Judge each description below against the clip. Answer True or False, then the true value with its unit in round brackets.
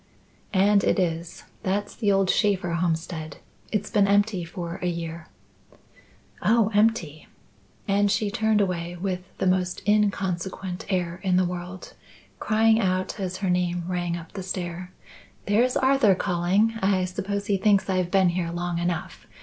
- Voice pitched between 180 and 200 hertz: True (185 Hz)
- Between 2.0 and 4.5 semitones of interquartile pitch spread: True (2.5 semitones)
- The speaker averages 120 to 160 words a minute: True (150 wpm)